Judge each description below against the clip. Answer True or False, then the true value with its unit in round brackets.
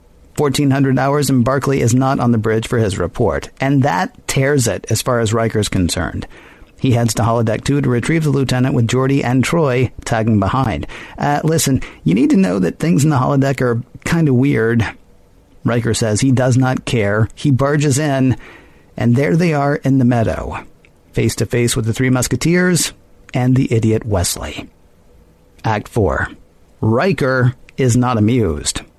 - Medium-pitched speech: False (125 Hz)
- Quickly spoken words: False (175 wpm)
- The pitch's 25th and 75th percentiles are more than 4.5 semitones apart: False (3.8 semitones)